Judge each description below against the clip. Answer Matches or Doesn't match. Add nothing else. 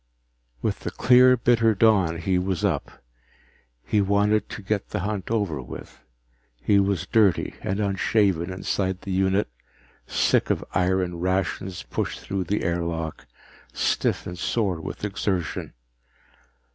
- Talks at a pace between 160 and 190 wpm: Doesn't match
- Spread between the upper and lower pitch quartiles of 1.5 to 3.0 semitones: Matches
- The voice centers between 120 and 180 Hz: Doesn't match